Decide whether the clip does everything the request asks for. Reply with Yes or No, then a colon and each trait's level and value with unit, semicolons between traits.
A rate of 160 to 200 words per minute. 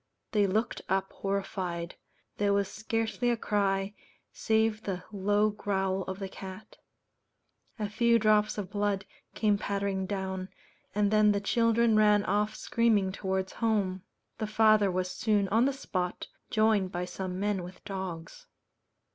No: average, 145 wpm